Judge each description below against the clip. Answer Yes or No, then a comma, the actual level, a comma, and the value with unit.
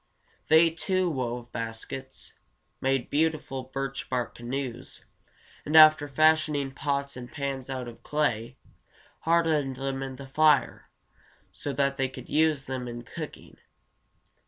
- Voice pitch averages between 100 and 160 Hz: Yes, low, 135 Hz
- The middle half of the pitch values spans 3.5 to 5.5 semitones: No, average, 3.0 semitones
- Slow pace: Yes, slow, 130 wpm